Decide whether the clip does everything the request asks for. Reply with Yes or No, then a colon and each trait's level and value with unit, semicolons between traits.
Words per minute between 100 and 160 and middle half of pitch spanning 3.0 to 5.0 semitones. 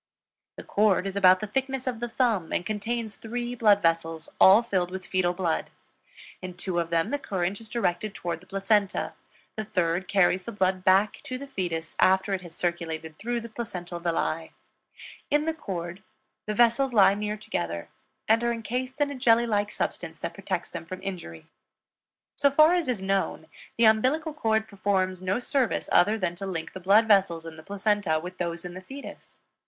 No: average, 190 wpm; average, 4.6 semitones